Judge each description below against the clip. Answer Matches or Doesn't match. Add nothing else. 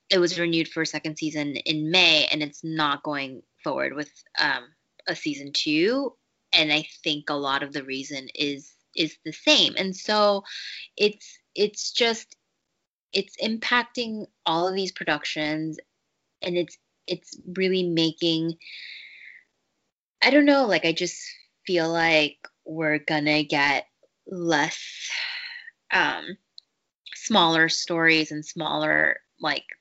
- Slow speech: Matches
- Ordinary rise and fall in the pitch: Matches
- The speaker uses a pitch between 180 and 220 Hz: Doesn't match